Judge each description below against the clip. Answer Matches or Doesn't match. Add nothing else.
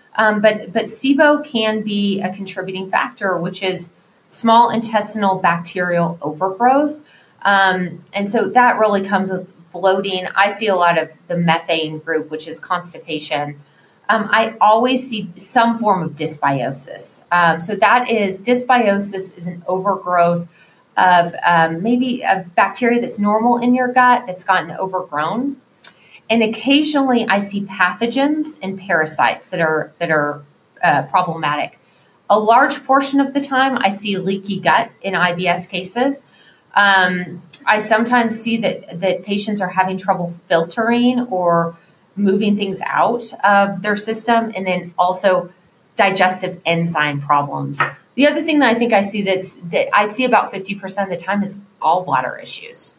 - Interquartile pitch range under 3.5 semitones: Doesn't match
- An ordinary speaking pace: Matches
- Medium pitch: Doesn't match